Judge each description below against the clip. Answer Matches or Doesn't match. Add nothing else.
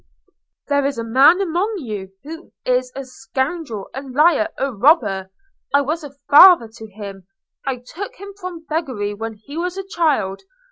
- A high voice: Matches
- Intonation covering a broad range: Matches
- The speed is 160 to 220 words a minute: Matches